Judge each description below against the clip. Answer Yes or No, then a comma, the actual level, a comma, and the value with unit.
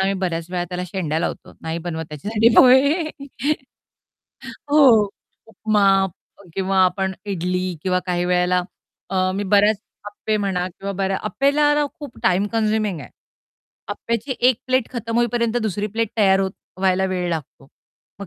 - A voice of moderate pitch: No, high, 200 Hz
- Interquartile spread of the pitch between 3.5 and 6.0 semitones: Yes, average, 4.0 semitones